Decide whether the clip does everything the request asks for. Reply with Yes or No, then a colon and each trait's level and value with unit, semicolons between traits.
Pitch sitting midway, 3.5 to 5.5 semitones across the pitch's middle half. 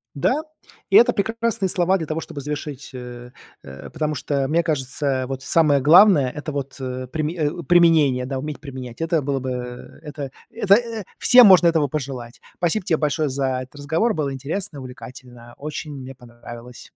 Yes: medium, 145 Hz; average, 4.1 semitones